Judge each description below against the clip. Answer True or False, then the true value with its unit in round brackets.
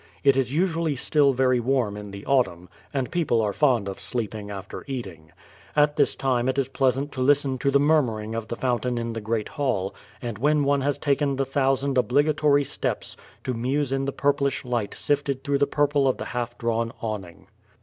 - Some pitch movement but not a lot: True (3.5 semitones)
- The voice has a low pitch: True (130 Hz)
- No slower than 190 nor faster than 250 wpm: True (200 wpm)